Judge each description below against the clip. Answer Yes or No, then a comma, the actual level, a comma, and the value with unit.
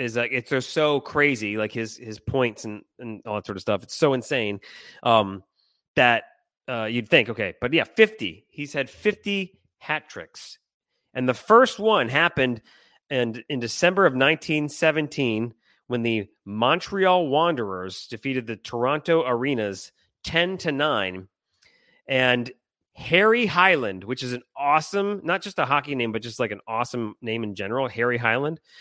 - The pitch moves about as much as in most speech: No, wide, 6.0 semitones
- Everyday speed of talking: Yes, average, 160 wpm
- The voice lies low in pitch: Yes, low, 125 Hz